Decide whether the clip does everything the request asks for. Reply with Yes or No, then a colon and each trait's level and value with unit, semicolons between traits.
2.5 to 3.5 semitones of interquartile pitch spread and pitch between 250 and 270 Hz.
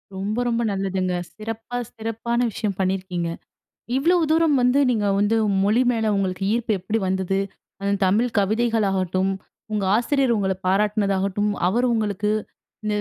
No: average, 3.2 semitones; high, 210 Hz